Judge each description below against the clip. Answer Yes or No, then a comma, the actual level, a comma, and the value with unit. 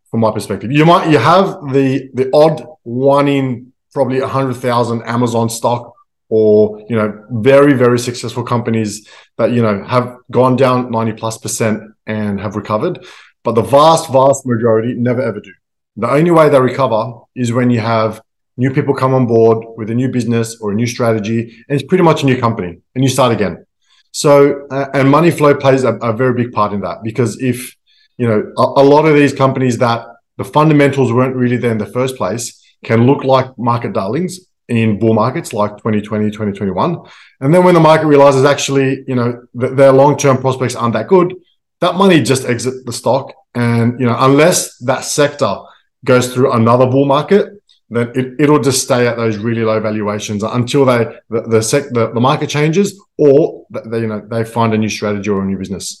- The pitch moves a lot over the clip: No, average, 3.4 semitones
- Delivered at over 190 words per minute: Yes, average, 200 wpm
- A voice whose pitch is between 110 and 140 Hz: Yes, low, 125 Hz